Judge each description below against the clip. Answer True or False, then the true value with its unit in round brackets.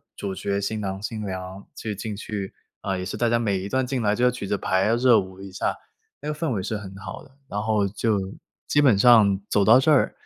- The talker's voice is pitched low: True (105 Hz)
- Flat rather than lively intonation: False (3.4 semitones)